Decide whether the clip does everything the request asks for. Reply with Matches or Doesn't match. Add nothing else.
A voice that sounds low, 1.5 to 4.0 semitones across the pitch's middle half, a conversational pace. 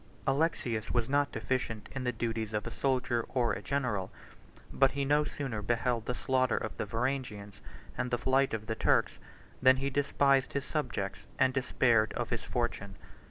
Matches